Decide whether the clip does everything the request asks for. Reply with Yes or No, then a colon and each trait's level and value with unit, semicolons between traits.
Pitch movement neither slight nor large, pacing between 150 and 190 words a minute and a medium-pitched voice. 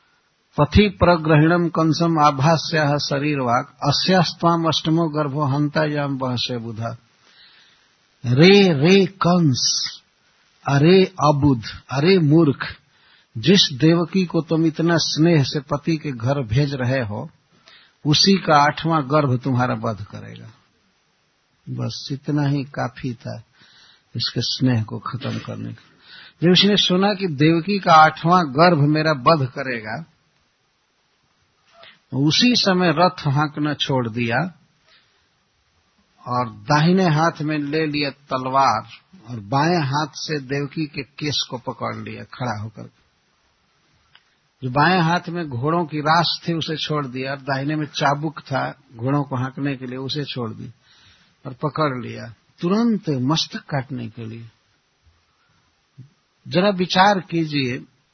No: average, 4.1 semitones; average, 125 wpm; medium, 150 Hz